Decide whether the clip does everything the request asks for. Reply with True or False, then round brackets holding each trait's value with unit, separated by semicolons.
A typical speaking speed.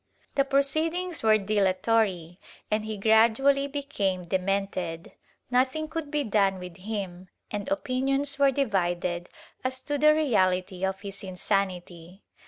False (130 wpm)